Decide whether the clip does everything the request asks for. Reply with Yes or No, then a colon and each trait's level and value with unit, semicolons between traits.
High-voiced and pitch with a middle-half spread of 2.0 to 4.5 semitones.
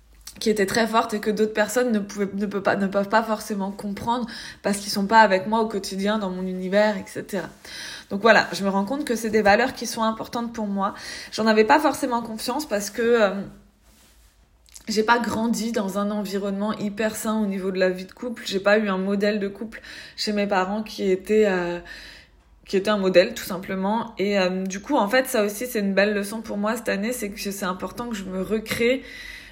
Yes: high, 210 Hz; narrow, 2.5 semitones